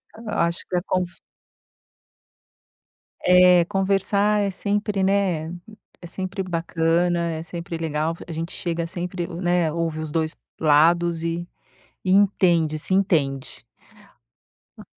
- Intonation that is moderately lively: No, narrow, 2.2 semitones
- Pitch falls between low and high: Yes, medium, 175 Hz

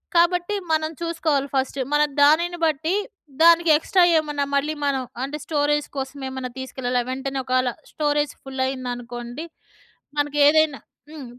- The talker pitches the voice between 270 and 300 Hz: Yes, very high, 290 Hz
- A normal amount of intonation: Yes, average, 3.1 semitones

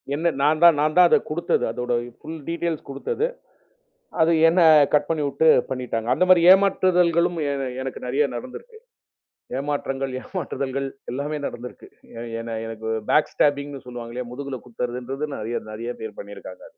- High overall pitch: No, medium, 140 Hz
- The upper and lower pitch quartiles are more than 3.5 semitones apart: Yes, average, 4.9 semitones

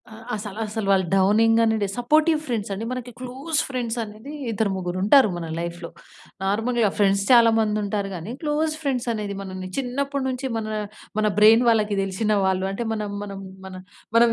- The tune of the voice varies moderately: Yes, average, 3.7 semitones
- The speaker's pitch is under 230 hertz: Yes, high, 220 Hz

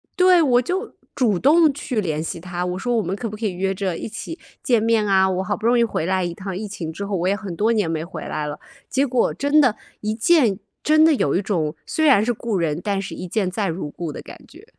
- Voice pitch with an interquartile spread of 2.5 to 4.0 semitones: No, average, 5.2 semitones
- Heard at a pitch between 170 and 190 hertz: No, high, 205 Hz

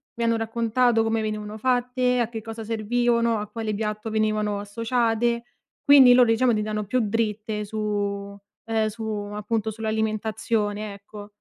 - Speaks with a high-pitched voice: Yes, high, 220 Hz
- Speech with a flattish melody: Yes, narrow, 1.6 semitones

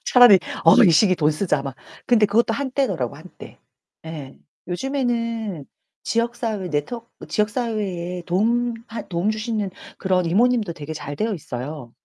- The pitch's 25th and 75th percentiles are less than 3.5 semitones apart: No, average, 5.3 semitones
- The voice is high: Yes, high, 210 Hz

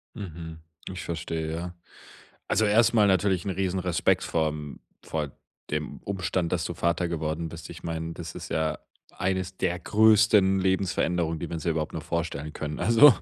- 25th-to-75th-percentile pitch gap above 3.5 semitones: No, average, 2.9 semitones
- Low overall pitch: Yes, very low, 85 Hz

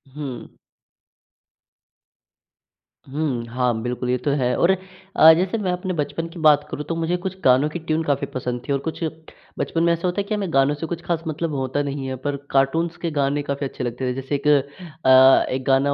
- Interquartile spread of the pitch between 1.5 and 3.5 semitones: No, average, 3.9 semitones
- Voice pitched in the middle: Yes, medium, 145 Hz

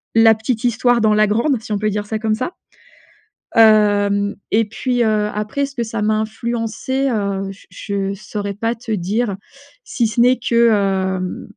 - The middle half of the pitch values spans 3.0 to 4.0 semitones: No, narrow, 2.4 semitones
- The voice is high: Yes, high, 215 Hz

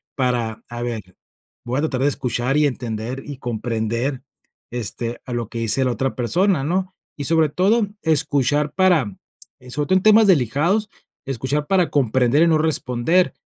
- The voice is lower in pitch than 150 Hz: Yes, low, 135 Hz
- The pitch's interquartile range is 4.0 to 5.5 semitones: Yes, average, 5.0 semitones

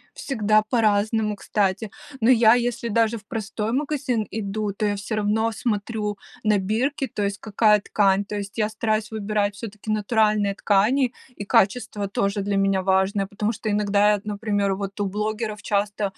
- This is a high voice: Yes, high, 210 Hz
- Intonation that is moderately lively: No, narrow, 1.5 semitones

